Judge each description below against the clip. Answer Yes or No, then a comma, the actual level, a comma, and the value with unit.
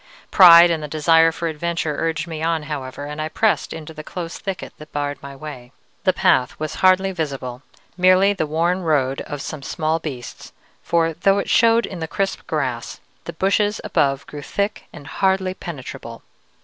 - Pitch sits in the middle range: Yes, medium, 160 Hz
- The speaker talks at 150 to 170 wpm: No, average, 180 wpm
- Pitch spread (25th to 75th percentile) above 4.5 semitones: No, average, 3.9 semitones